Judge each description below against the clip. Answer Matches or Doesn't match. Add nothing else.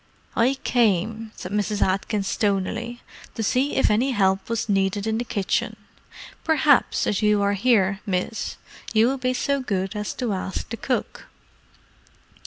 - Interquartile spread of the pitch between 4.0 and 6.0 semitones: Doesn't match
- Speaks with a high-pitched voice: Matches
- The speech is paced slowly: Doesn't match